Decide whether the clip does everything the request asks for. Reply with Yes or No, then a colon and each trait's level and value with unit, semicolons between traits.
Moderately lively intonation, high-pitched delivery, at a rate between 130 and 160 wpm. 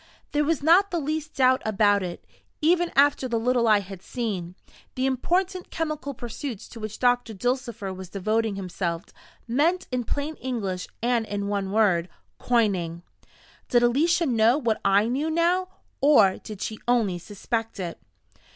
No: wide, 6.1 semitones; high, 235 Hz; average, 155 wpm